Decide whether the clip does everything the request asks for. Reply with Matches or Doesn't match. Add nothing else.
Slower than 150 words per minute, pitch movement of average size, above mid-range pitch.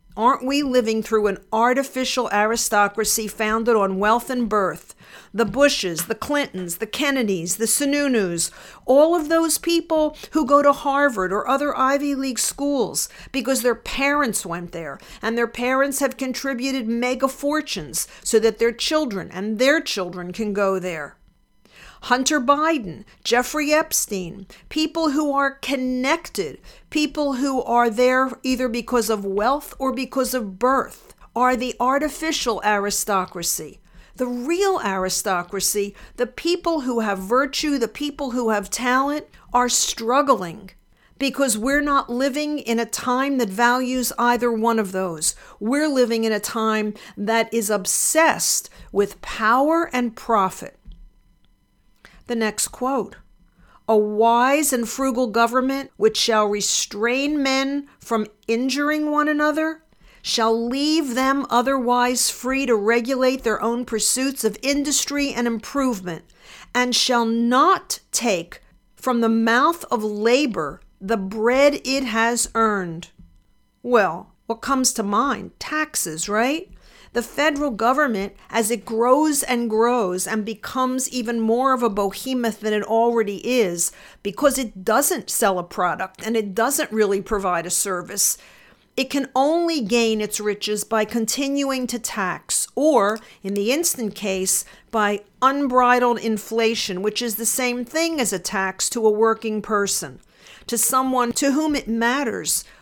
Matches